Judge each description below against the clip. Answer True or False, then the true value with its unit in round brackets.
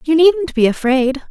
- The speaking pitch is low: False (295 Hz)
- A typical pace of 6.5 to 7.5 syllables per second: False (4.4 syllables/s)